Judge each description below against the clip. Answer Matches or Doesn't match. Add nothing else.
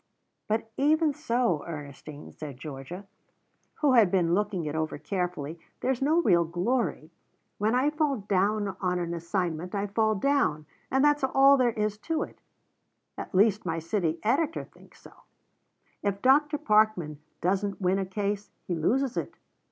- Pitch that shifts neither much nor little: Doesn't match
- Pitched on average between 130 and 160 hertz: Doesn't match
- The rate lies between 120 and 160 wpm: Matches